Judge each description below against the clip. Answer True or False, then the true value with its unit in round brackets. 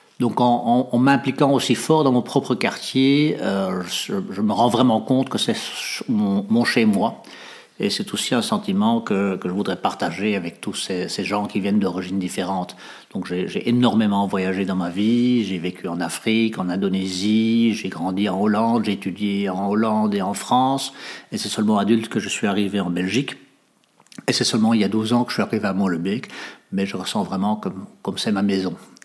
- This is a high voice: False (110 Hz)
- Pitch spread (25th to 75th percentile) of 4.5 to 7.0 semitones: True (5.1 semitones)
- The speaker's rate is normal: True (210 wpm)